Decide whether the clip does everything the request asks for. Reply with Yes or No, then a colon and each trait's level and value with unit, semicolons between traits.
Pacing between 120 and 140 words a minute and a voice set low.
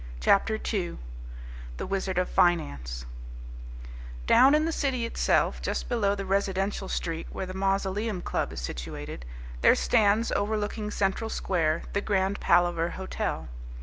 No: slow, 135 wpm; high, 195 Hz